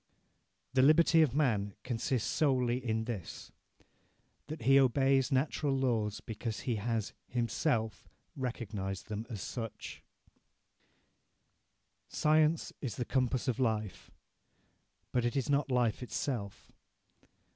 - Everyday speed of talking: No, slow, 115 wpm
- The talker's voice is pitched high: No, low, 125 Hz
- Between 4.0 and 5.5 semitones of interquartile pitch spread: No, average, 3.4 semitones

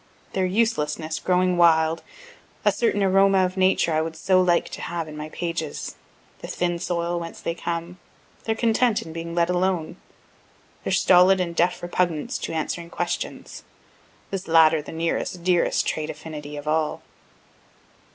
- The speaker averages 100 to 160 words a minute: Yes, average, 155 wpm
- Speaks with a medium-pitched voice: Yes, medium, 170 Hz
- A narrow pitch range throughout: Yes, narrow, 2.3 semitones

